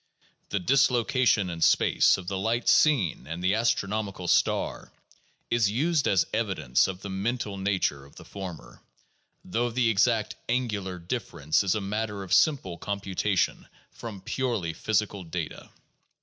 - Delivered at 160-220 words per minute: No, average, 140 wpm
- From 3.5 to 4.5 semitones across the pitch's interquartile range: Yes, average, 3.9 semitones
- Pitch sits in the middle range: No, low, 100 Hz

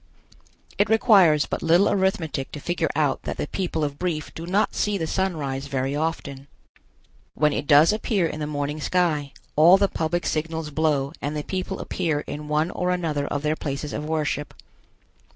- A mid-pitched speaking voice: Yes, medium, 155 Hz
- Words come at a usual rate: Yes, average, 185 wpm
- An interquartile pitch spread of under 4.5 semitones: Yes, average, 3.3 semitones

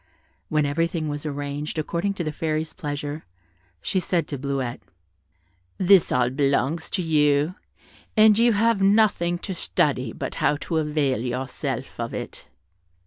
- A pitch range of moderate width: Yes, average, 3.6 semitones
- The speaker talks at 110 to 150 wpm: Yes, average, 140 wpm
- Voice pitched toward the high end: No, medium, 155 Hz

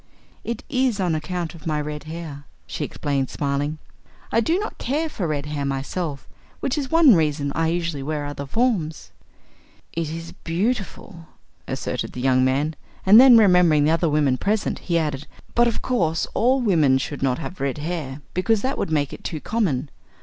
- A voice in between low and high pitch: Yes, medium, 160 Hz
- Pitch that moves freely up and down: Yes, wide, 5.9 semitones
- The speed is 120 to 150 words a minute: No, average, 180 wpm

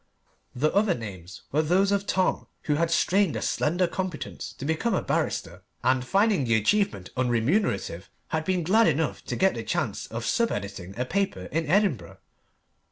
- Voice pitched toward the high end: No, medium, 160 Hz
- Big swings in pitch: Yes, wide, 8.3 semitones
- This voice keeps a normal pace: Yes, average, 170 wpm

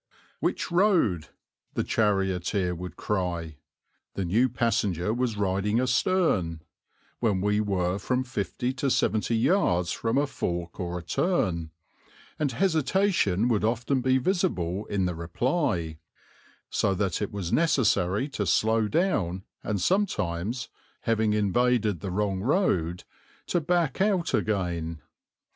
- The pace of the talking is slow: Yes, slow, 125 wpm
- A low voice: Yes, low, 105 Hz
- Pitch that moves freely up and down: Yes, wide, 6.3 semitones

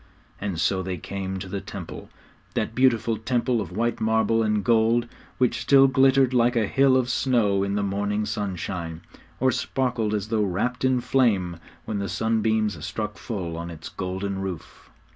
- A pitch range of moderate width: Yes, average, 3.7 semitones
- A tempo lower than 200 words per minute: Yes, average, 170 wpm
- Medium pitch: No, low, 110 Hz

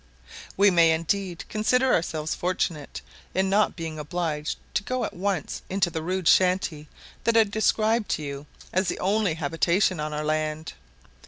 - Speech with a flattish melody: No, average, 4.3 semitones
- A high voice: No, medium, 175 Hz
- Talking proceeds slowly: No, average, 160 wpm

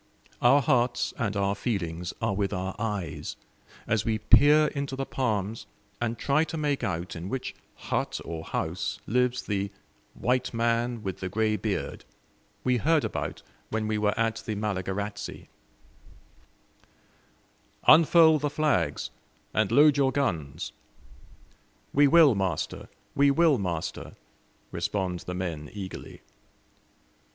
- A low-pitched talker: Yes, low, 110 Hz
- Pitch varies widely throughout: Yes, wide, 5.7 semitones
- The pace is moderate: No, slow, 130 wpm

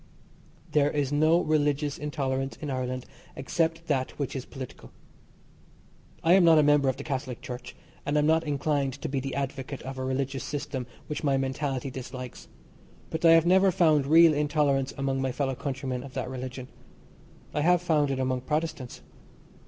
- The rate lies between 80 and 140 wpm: No, average, 175 wpm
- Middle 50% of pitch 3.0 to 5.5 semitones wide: No, narrow, 2.5 semitones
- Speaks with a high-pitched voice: No, medium, 140 Hz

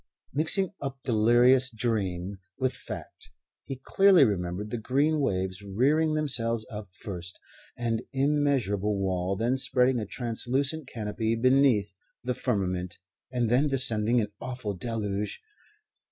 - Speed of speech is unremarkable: No, slow, 125 wpm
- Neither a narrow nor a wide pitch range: Yes, average, 4.5 semitones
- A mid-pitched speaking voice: No, low, 120 Hz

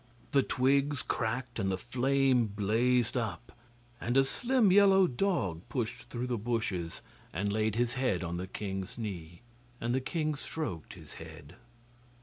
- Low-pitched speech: Yes, low, 120 Hz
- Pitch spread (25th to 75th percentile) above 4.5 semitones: Yes, average, 5.0 semitones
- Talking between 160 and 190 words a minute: No, average, 150 wpm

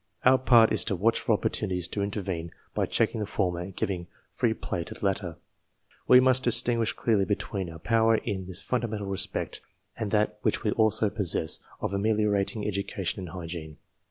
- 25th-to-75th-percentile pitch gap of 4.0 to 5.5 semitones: No, average, 3.2 semitones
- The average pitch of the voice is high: No, low, 100 Hz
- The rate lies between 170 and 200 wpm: Yes, average, 180 wpm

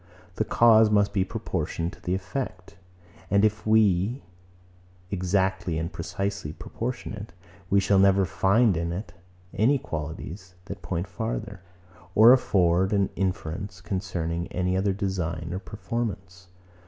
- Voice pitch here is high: No, very low, 95 Hz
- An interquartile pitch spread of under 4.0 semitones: Yes, average, 2.8 semitones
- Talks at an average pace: No, slow, 130 wpm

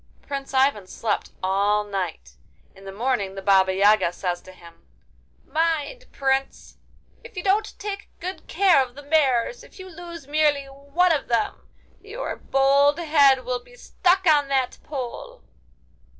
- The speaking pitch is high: Yes, very high, 275 Hz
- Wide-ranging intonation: Yes, wide, 7.9 semitones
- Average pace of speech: Yes, average, 150 wpm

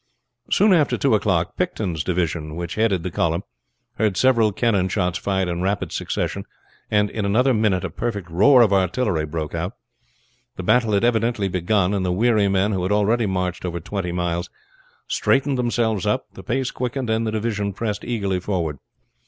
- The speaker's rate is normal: Yes, average, 175 wpm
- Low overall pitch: Yes, low, 100 Hz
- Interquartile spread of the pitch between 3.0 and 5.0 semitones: Yes, average, 4.1 semitones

